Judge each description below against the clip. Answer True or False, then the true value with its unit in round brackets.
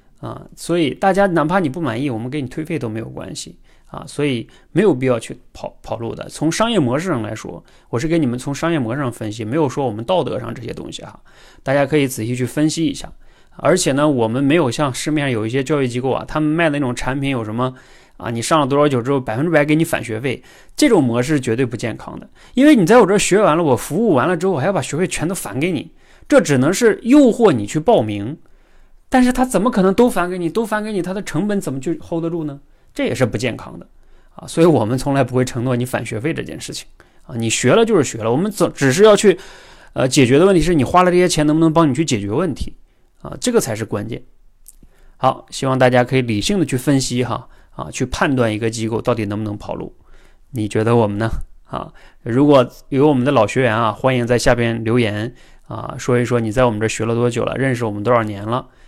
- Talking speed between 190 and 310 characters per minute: False (360 characters per minute)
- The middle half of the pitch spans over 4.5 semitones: True (5.5 semitones)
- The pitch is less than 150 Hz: True (135 Hz)